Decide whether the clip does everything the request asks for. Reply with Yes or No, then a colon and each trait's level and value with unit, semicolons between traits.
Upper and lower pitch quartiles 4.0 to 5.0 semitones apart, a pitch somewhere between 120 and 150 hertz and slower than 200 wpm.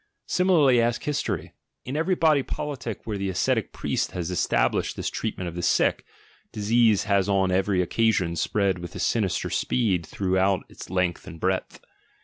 No: average, 4.5 semitones; low, 100 Hz; average, 160 wpm